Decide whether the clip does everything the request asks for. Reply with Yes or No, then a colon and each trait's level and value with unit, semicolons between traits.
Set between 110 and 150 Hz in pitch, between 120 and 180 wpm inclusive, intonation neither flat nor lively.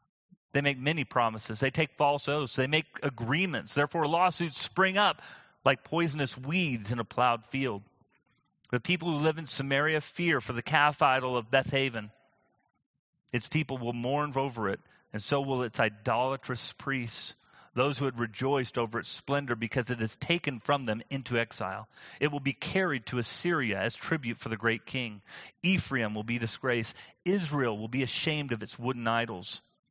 Yes: low, 135 Hz; average, 175 wpm; average, 4.0 semitones